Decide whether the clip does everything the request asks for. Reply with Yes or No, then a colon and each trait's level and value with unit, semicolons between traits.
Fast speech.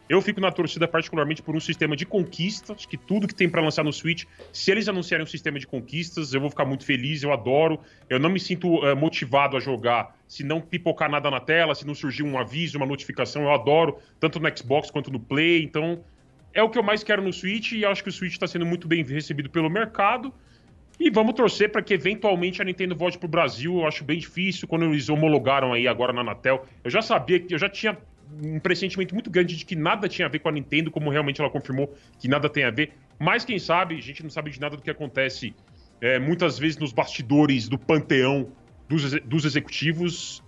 Yes: fast, 230 wpm